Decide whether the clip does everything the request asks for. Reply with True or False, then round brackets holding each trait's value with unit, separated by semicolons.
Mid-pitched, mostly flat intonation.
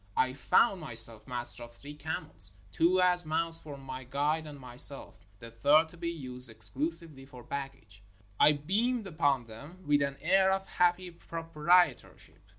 False (145 Hz; 5.0 semitones)